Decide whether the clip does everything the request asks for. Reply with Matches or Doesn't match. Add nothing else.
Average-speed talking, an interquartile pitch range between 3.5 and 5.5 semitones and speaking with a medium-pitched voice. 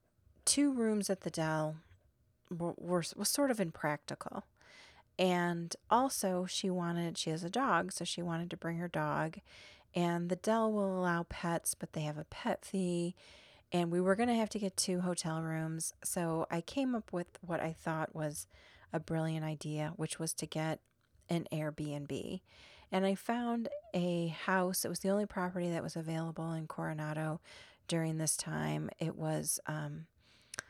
Doesn't match